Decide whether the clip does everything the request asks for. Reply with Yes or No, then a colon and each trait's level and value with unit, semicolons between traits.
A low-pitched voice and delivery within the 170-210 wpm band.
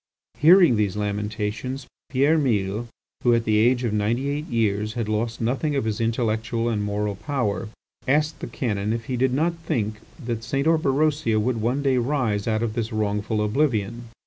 Yes: low, 115 Hz; average, 175 wpm